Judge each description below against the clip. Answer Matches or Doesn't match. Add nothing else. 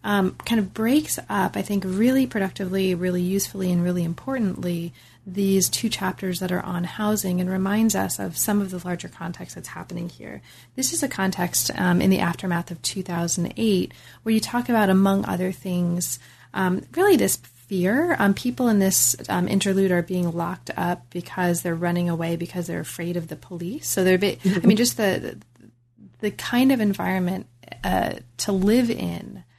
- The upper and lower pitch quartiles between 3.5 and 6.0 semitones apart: Doesn't match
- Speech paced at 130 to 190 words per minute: Matches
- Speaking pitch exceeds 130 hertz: Matches